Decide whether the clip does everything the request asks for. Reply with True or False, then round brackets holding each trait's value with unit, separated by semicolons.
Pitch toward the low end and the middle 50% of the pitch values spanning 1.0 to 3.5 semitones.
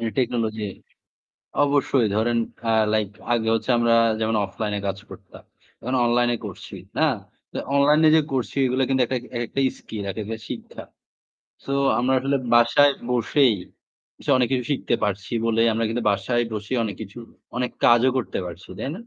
True (120 Hz; 2.8 semitones)